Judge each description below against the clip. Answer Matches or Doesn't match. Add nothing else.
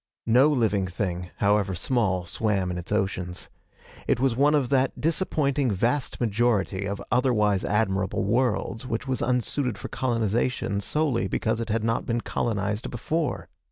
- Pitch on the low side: Matches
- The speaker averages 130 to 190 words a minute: Matches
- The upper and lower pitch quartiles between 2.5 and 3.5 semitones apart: Doesn't match